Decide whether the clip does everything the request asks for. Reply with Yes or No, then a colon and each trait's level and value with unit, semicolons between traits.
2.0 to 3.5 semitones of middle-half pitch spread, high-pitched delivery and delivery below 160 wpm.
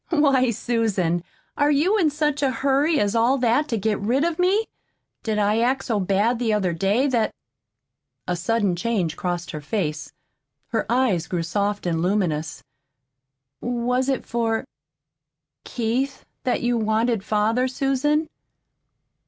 No: average, 4.9 semitones; high, 230 Hz; average, 145 wpm